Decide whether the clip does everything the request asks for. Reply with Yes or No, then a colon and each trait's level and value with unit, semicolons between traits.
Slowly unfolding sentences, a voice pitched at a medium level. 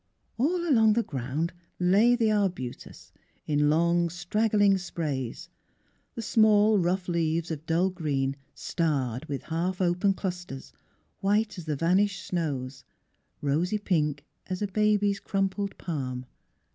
Yes: slow, 125 wpm; medium, 175 Hz